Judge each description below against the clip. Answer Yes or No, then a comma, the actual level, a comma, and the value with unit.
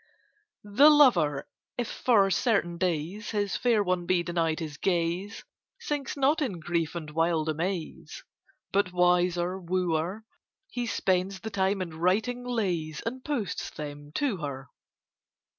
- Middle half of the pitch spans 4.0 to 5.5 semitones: Yes, average, 4.9 semitones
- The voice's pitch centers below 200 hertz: Yes, medium, 185 Hz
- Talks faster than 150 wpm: No, slow, 135 wpm